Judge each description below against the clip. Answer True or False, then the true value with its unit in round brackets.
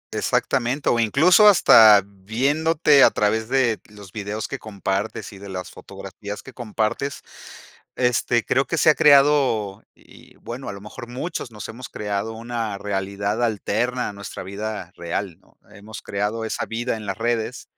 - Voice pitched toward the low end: True (110 Hz)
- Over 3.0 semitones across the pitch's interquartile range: True (3.7 semitones)